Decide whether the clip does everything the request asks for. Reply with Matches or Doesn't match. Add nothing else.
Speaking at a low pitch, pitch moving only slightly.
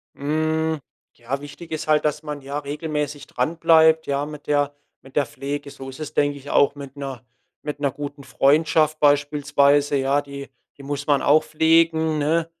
Doesn't match